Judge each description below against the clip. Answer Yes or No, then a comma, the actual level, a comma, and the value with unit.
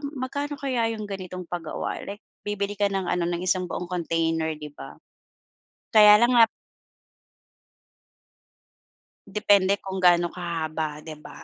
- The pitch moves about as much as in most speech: Yes, average, 3.6 semitones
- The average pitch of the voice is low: No, medium, 185 Hz